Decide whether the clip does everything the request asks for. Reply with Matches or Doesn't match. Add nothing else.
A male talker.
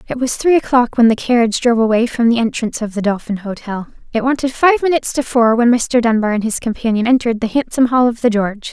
Doesn't match